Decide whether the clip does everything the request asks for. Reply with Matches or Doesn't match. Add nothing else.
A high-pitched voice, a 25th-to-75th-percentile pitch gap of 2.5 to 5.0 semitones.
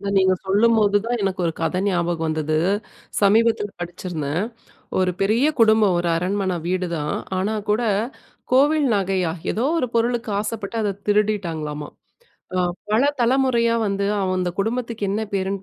Matches